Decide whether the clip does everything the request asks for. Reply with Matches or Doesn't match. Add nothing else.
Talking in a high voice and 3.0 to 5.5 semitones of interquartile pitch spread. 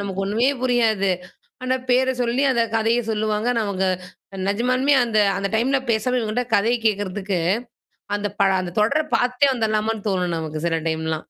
Matches